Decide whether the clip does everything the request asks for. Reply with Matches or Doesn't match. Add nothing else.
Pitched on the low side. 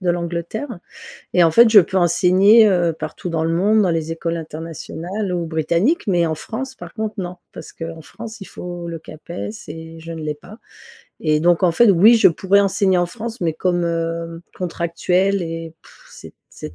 Doesn't match